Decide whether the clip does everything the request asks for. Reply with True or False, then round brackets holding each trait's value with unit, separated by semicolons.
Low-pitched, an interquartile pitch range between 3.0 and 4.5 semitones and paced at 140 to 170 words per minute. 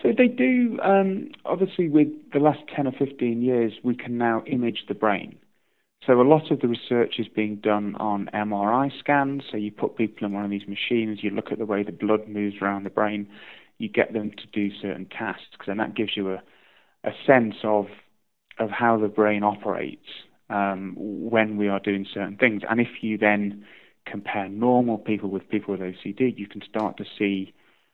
False (110 Hz; 3.4 semitones; 200 wpm)